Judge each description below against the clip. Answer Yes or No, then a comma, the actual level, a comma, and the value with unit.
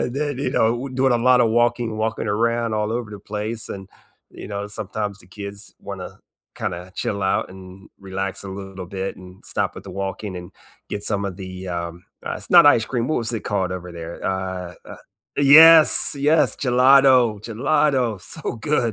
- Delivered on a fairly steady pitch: No, average, 4.1 semitones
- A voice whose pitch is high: No, low, 105 Hz